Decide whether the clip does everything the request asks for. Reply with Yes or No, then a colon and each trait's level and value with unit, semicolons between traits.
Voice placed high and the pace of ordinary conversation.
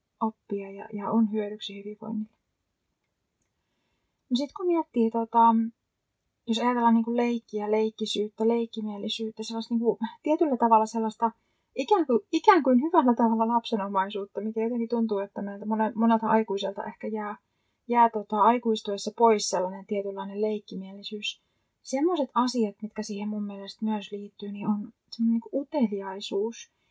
Yes: high, 220 Hz; average, 135 wpm